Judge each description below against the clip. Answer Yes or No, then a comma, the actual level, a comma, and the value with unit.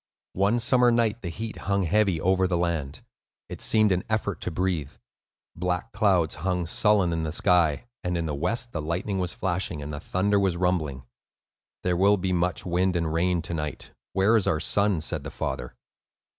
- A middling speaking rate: Yes, average, 190 wpm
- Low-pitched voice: Yes, very low, 90 Hz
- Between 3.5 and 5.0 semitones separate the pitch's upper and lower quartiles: No, average, 3.1 semitones